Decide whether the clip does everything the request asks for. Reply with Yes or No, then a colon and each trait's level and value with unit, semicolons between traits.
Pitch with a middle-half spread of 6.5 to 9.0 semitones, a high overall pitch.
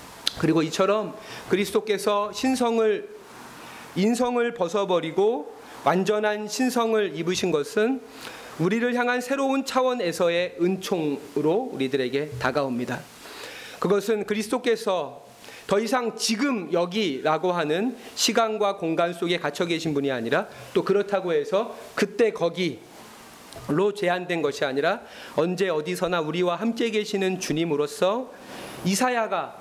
No: average, 5.2 semitones; high, 200 Hz